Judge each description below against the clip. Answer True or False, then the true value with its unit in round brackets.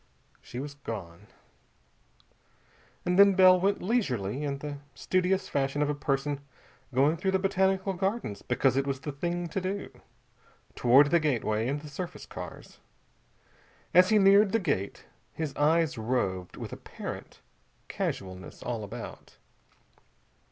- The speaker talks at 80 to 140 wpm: True (135 wpm)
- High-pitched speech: False (150 Hz)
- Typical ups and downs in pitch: False (6.4 semitones)